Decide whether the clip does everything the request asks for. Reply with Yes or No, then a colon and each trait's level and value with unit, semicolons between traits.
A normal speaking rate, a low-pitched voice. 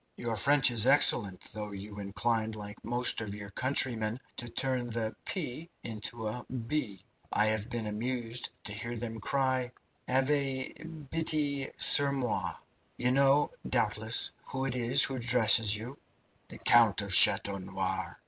Yes: average, 150 wpm; low, 120 Hz